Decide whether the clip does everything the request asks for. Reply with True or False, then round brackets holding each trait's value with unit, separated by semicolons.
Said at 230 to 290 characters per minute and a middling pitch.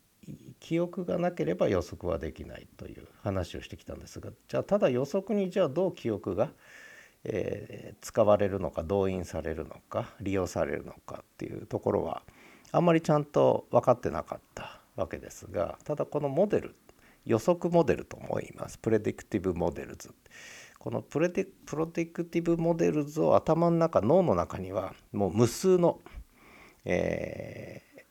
False (325 characters per minute; 160 Hz)